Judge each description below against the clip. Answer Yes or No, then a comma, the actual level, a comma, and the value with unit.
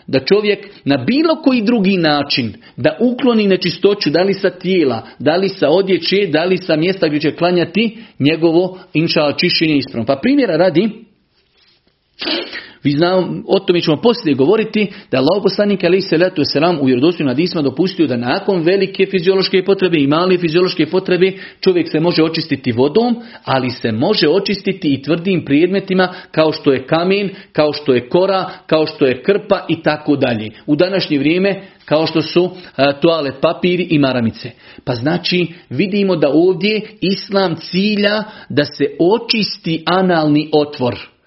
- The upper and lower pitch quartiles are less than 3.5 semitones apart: No, average, 4.3 semitones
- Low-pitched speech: No, medium, 175 Hz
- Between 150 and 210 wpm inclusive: Yes, average, 155 wpm